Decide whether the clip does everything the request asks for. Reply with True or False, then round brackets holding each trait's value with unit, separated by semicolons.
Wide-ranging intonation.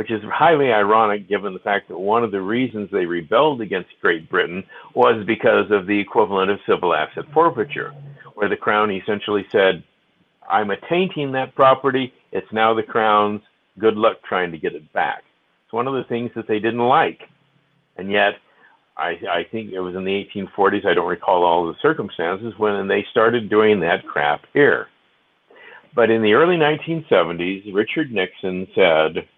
False (3.6 semitones)